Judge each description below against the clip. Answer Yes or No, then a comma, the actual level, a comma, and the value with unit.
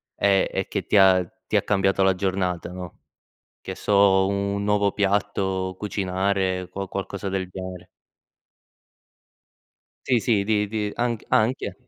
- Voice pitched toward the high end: No, low, 100 Hz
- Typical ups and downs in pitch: No, narrow, 1.5 semitones